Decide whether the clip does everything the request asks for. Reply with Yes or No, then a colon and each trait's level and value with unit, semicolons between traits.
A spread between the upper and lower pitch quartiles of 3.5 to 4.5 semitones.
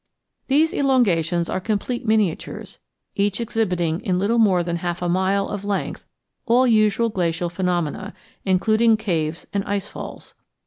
Yes: average, 3.8 semitones